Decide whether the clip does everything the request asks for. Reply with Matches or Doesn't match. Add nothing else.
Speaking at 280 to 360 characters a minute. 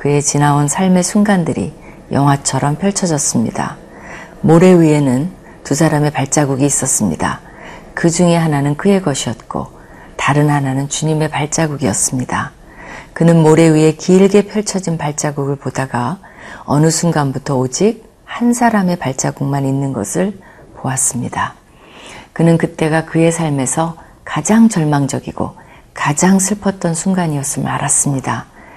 Matches